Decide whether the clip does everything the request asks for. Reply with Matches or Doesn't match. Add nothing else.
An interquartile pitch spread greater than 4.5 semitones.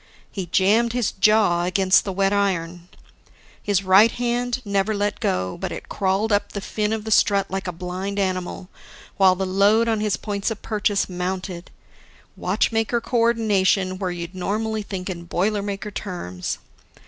Doesn't match